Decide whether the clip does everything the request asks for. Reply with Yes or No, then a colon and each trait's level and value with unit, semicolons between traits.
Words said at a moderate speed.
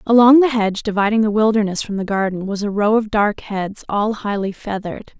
No: fast, 210 wpm